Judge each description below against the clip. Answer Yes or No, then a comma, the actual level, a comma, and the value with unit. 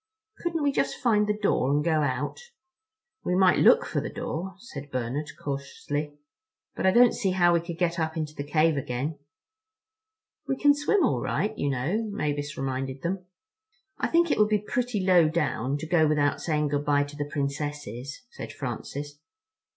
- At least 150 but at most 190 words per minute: Yes, average, 180 wpm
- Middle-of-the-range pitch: Yes, medium, 155 Hz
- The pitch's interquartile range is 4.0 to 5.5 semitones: Yes, average, 5.0 semitones